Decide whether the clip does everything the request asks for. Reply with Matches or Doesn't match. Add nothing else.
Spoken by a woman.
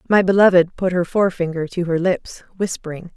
Matches